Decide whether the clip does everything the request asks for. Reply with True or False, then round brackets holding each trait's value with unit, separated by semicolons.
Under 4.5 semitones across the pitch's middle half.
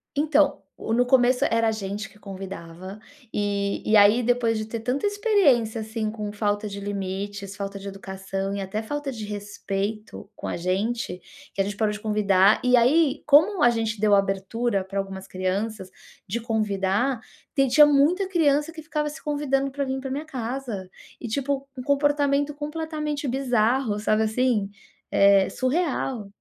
False (5.5 semitones)